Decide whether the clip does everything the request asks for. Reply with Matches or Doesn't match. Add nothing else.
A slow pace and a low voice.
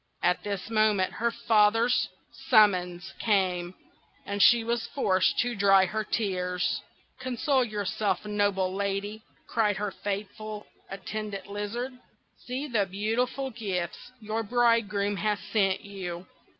Doesn't match